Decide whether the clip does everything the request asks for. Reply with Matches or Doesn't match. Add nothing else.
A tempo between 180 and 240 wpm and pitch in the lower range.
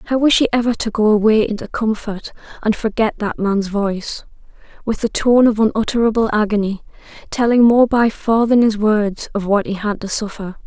Doesn't match